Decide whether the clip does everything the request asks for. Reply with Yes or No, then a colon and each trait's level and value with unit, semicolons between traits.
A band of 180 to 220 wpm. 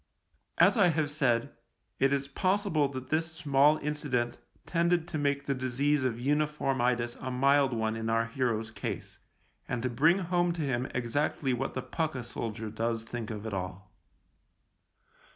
No: average, 170 wpm